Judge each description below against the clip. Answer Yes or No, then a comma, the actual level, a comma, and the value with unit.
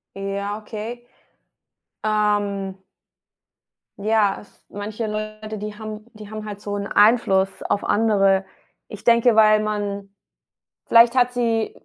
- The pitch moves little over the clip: Yes, narrow, 1.4 semitones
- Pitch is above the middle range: Yes, high, 210 Hz